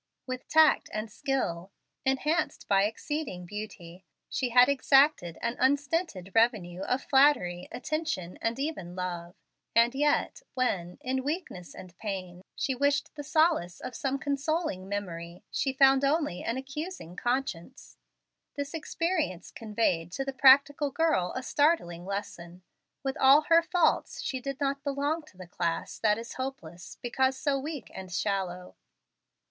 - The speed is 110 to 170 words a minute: Yes, average, 140 wpm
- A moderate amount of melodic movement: No, wide, 7.5 semitones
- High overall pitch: Yes, very high, 255 Hz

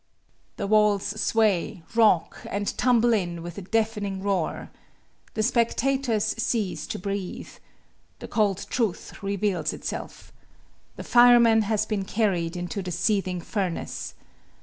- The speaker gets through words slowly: Yes, slow, 125 wpm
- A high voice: Yes, high, 205 Hz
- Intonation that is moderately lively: Yes, average, 3.3 semitones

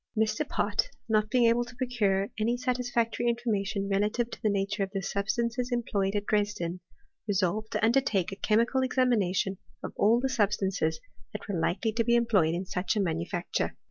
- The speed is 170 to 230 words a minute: Yes, average, 185 wpm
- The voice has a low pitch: No, high, 215 Hz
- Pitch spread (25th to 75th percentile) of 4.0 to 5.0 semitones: No, average, 3.4 semitones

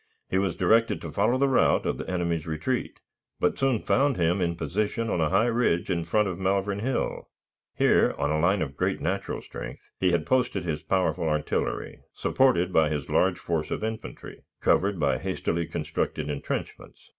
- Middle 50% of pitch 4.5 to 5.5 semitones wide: Yes, average, 5.1 semitones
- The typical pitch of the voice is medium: No, very low, 90 Hz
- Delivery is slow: No, average, 180 wpm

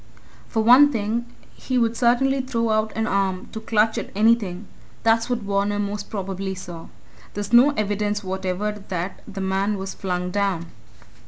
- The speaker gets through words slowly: No, average, 160 wpm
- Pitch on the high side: Yes, high, 205 Hz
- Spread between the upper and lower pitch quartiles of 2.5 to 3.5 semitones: Yes, average, 3.0 semitones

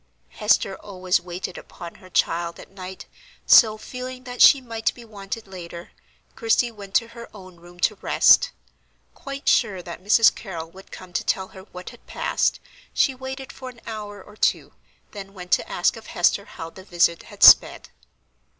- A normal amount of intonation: Yes, average, 4.2 semitones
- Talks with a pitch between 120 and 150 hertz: No, high, 195 Hz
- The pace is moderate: Yes, average, 175 wpm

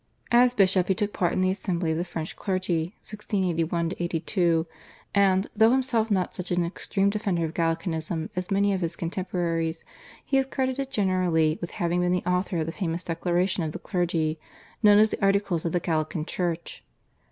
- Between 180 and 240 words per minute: Yes, average, 185 wpm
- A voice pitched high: No, medium, 180 Hz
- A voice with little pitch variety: No, average, 3.0 semitones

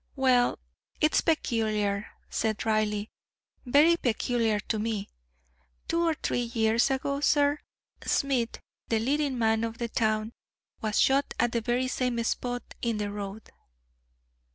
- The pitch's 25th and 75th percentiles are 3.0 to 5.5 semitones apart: Yes, average, 3.5 semitones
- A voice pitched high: Yes, high, 235 Hz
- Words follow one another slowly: Yes, slow, 130 wpm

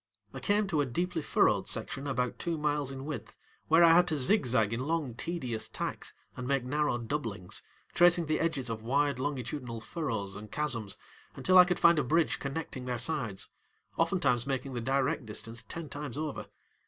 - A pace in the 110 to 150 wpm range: No, average, 180 wpm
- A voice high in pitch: No, medium, 140 Hz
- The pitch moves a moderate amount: Yes, average, 4.8 semitones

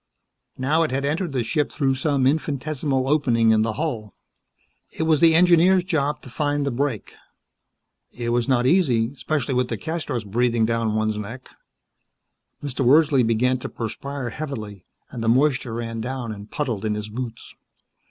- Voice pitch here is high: No, low, 130 Hz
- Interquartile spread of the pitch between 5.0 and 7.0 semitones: No, average, 4.3 semitones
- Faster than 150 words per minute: Yes, average, 160 wpm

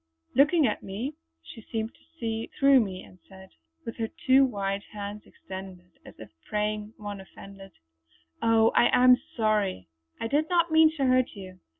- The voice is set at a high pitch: Yes, high, 220 Hz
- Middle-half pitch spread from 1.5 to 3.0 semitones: No, average, 4.7 semitones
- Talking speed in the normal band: Yes, average, 170 wpm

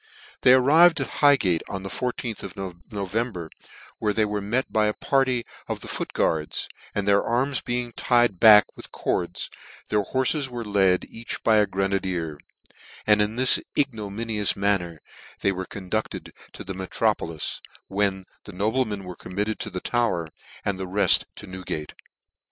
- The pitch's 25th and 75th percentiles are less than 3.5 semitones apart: No, average, 3.8 semitones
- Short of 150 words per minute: No, average, 165 wpm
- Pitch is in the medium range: No, low, 105 Hz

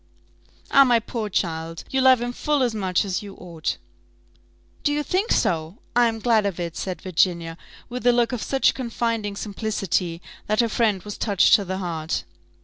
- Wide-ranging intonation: No, average, 4.9 semitones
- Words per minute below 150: No, average, 185 wpm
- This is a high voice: Yes, high, 210 Hz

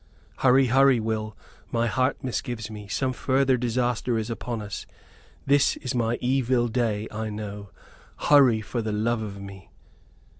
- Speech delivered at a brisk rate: No, average, 150 wpm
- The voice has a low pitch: Yes, low, 115 Hz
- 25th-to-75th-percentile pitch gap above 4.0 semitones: No, average, 2.9 semitones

